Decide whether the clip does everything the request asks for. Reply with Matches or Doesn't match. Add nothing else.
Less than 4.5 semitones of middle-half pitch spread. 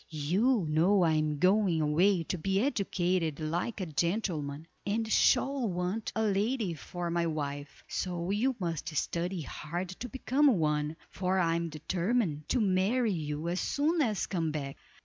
Doesn't match